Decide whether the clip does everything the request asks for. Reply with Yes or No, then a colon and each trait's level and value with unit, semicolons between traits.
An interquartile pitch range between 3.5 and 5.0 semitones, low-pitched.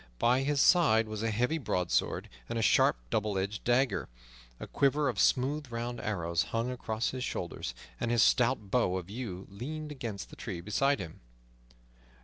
Yes: average, 4.5 semitones; low, 115 Hz